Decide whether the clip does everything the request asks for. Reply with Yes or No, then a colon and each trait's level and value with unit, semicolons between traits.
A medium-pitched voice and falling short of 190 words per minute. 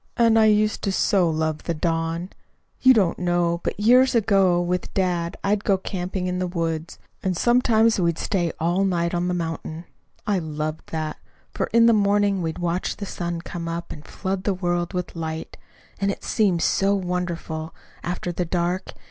Yes: medium, 180 Hz; average, 180 wpm